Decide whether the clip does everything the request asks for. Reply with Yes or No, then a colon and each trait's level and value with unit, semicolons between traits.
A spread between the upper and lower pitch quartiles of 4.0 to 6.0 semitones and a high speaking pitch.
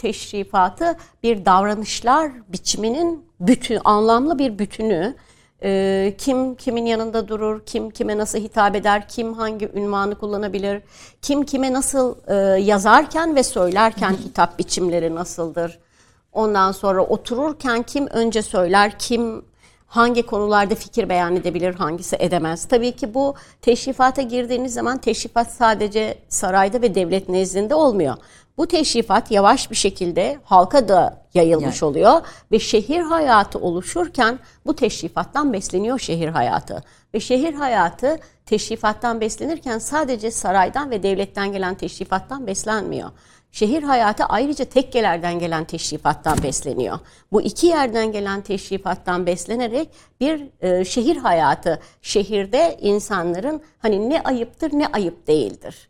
Yes: average, 4.8 semitones; high, 220 Hz